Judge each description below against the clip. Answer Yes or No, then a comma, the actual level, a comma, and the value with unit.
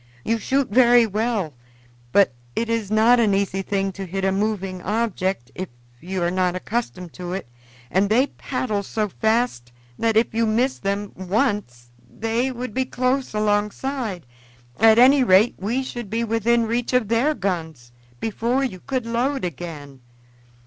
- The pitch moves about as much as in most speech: Yes, average, 4.0 semitones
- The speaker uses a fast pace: No, average, 160 wpm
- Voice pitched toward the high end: Yes, high, 215 Hz